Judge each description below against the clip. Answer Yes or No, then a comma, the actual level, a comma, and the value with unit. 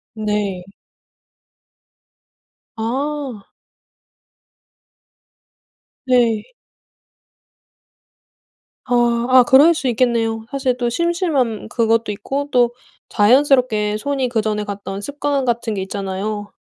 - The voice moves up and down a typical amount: Yes, average, 3.8 semitones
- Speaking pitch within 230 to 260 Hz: Yes, high, 235 Hz